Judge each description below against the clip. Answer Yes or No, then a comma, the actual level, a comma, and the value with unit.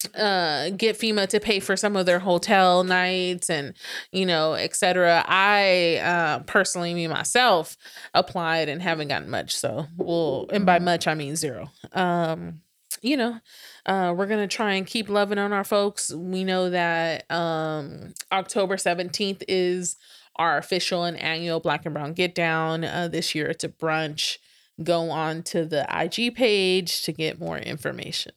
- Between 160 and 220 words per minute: Yes, average, 165 wpm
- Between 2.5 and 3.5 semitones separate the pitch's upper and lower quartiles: Yes, average, 2.8 semitones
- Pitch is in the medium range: Yes, medium, 175 Hz